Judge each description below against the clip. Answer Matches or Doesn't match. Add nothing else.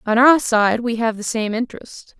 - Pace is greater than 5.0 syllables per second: Doesn't match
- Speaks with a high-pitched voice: Matches